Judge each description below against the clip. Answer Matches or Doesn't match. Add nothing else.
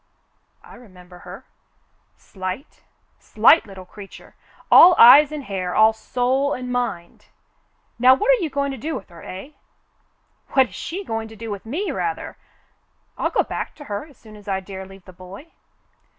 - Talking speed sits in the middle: Matches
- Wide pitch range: Matches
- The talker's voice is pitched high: Matches